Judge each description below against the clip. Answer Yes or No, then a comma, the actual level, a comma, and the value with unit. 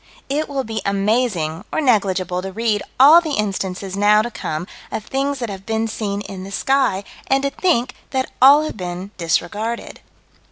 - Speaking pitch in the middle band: No, high, 215 Hz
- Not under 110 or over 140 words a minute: No, average, 175 wpm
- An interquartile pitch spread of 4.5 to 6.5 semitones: Yes, wide, 5.4 semitones